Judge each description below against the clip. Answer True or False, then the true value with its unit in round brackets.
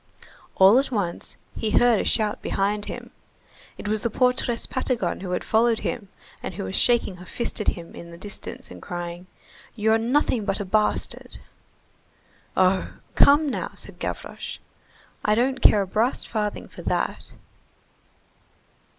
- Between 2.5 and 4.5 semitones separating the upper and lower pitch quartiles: True (3.9 semitones)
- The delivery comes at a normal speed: True (155 wpm)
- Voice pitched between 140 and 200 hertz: False (210 Hz)